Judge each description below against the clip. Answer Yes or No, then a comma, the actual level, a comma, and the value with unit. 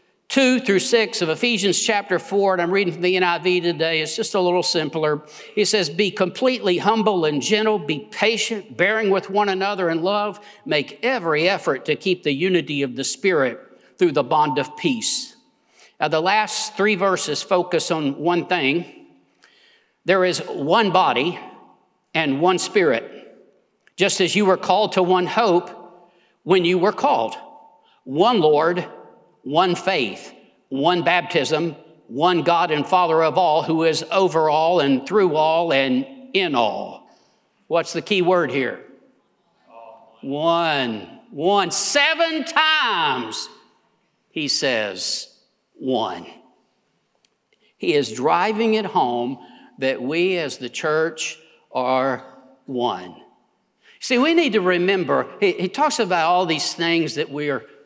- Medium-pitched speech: Yes, medium, 180 Hz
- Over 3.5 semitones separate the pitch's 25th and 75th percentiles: Yes, average, 5.1 semitones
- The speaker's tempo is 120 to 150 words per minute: Yes, average, 145 wpm